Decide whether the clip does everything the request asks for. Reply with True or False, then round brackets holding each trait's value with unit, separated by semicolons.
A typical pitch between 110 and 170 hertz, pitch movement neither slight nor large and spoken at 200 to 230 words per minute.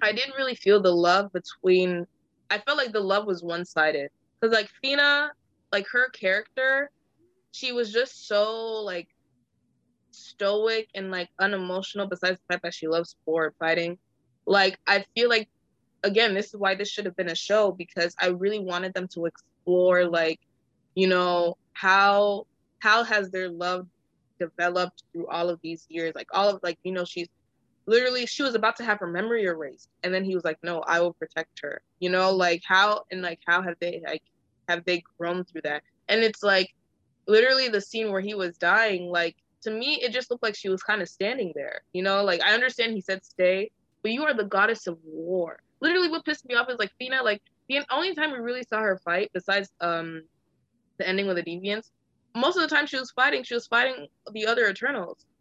False (195 Hz; 4.2 semitones; 205 wpm)